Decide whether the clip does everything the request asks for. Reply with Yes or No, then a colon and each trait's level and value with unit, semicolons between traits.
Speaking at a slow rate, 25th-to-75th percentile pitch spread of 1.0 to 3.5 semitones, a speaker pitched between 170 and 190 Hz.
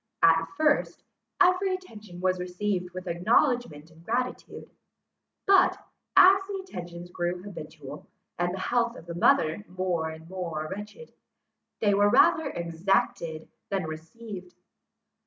No: slow, 125 wpm; wide, 5.5 semitones; medium, 185 Hz